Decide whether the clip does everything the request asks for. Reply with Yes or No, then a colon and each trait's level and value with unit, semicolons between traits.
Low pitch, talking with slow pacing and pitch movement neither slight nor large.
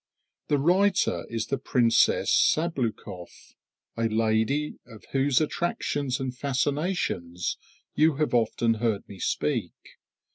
Yes: low, 130 Hz; slow, 110 wpm; average, 4.9 semitones